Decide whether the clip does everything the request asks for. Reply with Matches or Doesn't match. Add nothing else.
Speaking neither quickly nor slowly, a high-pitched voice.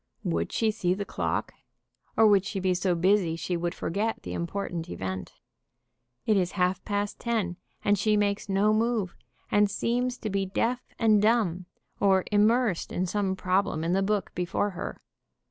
Matches